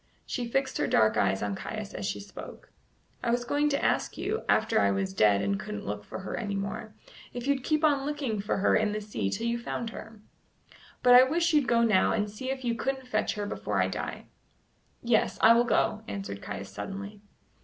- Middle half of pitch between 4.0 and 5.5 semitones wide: Yes, average, 4.5 semitones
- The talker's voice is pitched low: No, high, 220 Hz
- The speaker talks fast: Yes, fast, 220 wpm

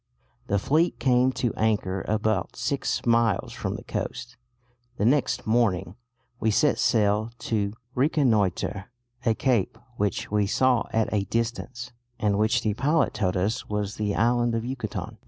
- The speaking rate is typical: Yes, average, 150 wpm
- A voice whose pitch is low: Yes, low, 110 Hz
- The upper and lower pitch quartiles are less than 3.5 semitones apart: Yes, average, 3.0 semitones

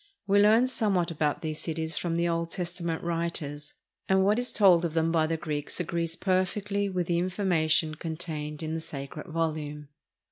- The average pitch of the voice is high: No, medium, 165 Hz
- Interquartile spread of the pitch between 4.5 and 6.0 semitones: No, average, 2.8 semitones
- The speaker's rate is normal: Yes, average, 175 wpm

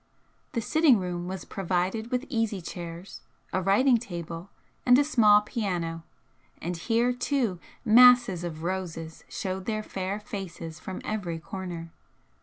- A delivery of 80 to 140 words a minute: Yes, slow, 135 wpm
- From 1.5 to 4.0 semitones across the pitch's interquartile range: No, average, 4.6 semitones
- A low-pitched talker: No, high, 190 Hz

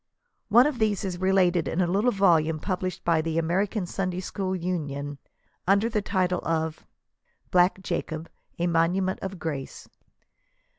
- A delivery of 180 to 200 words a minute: No, average, 145 wpm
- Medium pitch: Yes, medium, 180 Hz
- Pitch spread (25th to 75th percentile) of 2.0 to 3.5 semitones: Yes, average, 2.8 semitones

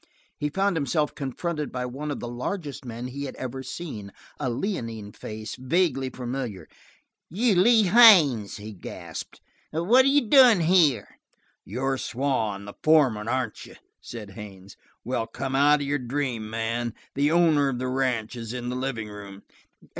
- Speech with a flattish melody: No, average, 5.2 semitones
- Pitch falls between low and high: No, low, 130 Hz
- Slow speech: No, average, 160 wpm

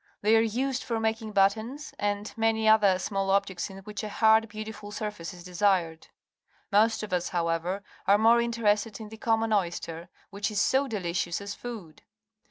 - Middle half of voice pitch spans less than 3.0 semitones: Yes, narrow, 2.6 semitones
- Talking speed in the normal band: Yes, average, 175 wpm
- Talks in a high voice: Yes, high, 210 Hz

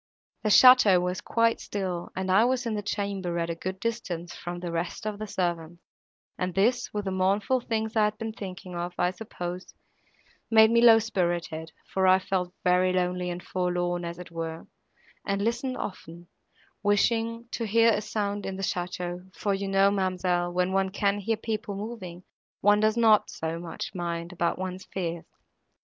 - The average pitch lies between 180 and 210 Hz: Yes, high, 190 Hz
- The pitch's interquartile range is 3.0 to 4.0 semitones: Yes, average, 3.3 semitones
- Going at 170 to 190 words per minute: Yes, average, 180 wpm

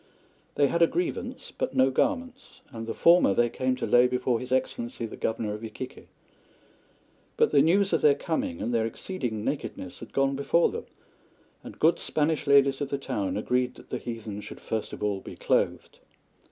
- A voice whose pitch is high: No, low, 130 Hz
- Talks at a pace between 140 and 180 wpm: No, average, 190 wpm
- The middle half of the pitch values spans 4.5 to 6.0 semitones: Yes, average, 4.9 semitones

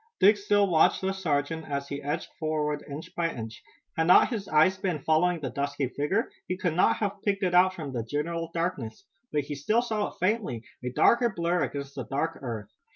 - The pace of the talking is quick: Yes, fast, 210 wpm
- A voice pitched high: No, medium, 160 Hz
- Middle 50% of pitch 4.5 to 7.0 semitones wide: Yes, average, 4.9 semitones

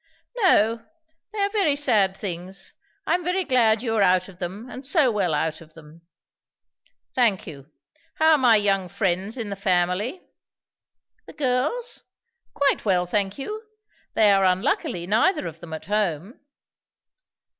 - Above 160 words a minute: No, average, 155 wpm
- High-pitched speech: Yes, high, 210 Hz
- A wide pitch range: Yes, wide, 6.8 semitones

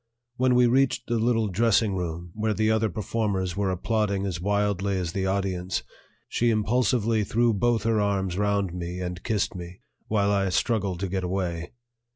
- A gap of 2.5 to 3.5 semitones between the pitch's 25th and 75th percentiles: Yes, average, 3.2 semitones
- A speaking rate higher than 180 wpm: No, average, 175 wpm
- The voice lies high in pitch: No, low, 100 Hz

